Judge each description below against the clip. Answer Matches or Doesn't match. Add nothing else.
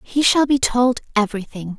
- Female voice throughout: Matches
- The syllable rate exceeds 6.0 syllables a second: Doesn't match